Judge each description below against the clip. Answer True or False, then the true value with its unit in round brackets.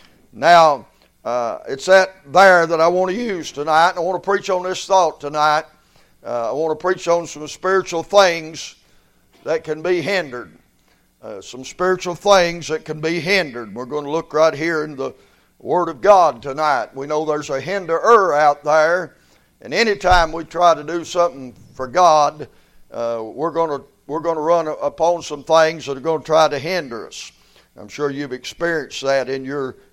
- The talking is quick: False (190 wpm)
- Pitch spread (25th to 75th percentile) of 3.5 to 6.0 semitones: False (3.1 semitones)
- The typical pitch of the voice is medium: True (160 Hz)